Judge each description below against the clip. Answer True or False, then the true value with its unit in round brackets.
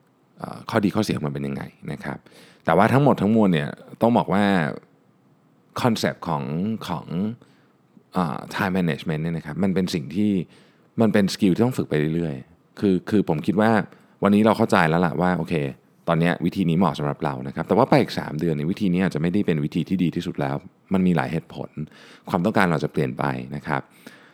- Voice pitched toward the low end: True (85 Hz)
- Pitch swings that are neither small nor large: True (4.2 semitones)